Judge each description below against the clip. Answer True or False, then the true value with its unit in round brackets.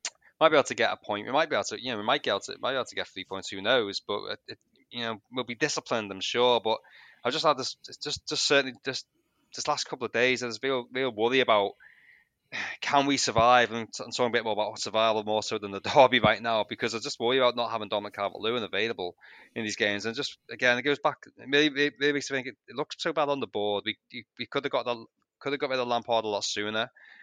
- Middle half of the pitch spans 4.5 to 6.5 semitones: False (4.1 semitones)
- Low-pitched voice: True (120 Hz)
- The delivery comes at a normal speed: False (260 wpm)